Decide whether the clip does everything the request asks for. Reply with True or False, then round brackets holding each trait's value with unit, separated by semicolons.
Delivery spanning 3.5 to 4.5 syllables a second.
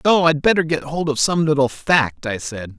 False (4.8 syllables/s)